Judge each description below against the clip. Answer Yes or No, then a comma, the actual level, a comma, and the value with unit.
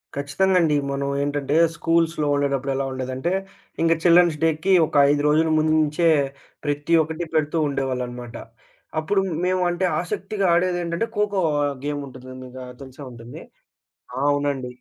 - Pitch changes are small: No, average, 3.7 semitones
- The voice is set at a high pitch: No, medium, 150 Hz